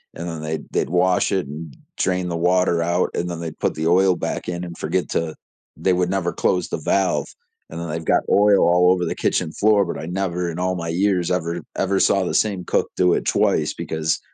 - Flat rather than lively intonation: Yes, narrow, 1.8 semitones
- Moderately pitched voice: No, very low, 90 Hz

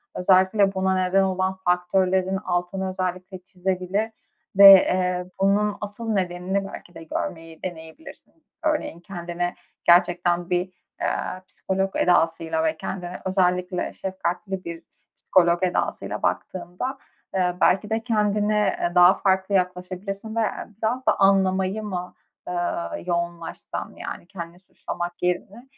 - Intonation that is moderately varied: No, narrow, 1.7 semitones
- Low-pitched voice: No, medium, 185 Hz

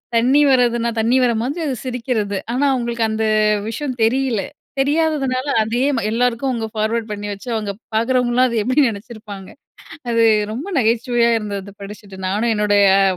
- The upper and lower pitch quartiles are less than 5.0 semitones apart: Yes, average, 2.9 semitones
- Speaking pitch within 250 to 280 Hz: No, high, 235 Hz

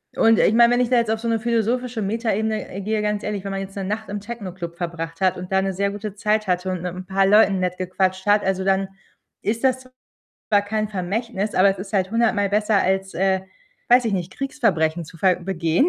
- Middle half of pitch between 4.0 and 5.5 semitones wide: No, average, 2.8 semitones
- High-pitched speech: Yes, high, 200 Hz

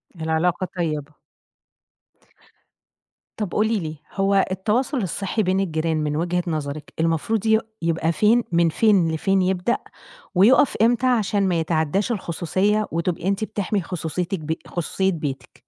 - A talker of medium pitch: Yes, medium, 180 Hz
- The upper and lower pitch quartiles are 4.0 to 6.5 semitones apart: Yes, average, 4.3 semitones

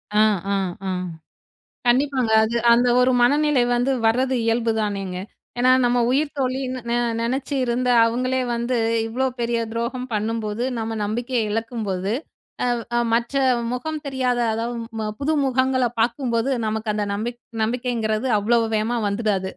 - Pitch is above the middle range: Yes, high, 240 Hz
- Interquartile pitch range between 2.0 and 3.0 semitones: Yes, narrow, 2.4 semitones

